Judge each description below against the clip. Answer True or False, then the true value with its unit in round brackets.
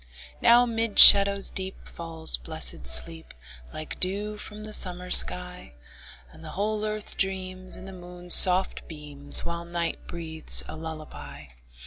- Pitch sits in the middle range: True (180 Hz)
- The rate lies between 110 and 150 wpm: True (140 wpm)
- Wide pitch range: False (3.8 semitones)